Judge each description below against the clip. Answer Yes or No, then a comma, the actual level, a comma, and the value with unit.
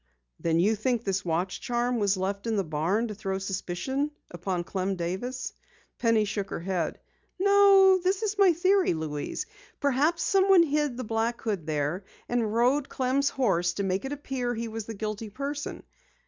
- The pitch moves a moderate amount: No, wide, 6.6 semitones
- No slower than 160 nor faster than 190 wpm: Yes, average, 175 wpm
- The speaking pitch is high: Yes, high, 225 Hz